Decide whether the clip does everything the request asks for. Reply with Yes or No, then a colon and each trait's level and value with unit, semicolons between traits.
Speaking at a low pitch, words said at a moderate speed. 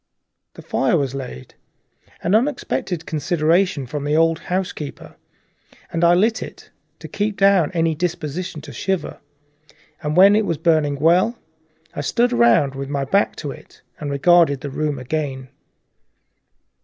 No: medium, 160 Hz; average, 145 wpm